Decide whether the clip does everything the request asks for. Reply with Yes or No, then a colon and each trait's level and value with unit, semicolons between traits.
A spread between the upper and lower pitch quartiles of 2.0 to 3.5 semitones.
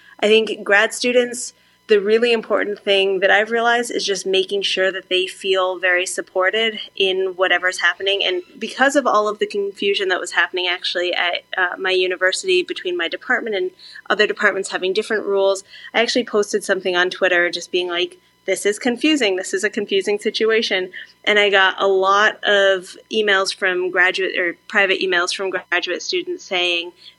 Yes: average, 2.9 semitones